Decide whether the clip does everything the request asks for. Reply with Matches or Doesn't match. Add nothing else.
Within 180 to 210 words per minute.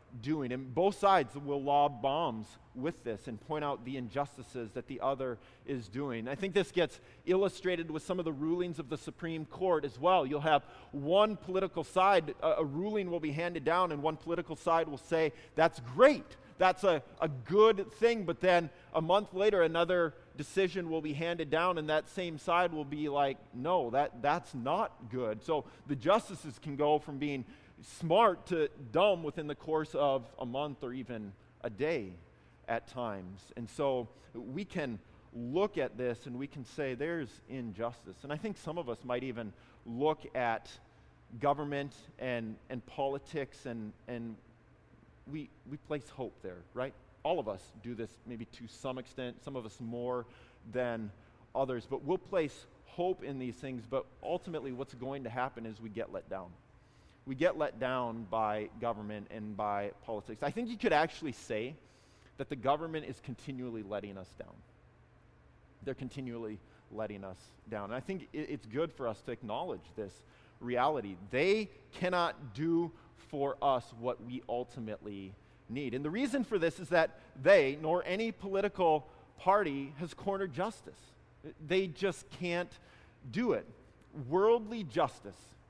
Doesn't match